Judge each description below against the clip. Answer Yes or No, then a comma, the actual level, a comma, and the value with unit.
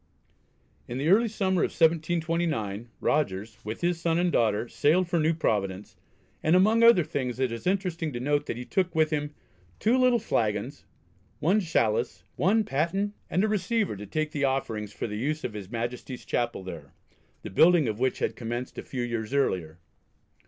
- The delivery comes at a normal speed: Yes, average, 180 wpm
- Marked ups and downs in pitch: Yes, wide, 7.2 semitones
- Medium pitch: Yes, medium, 145 Hz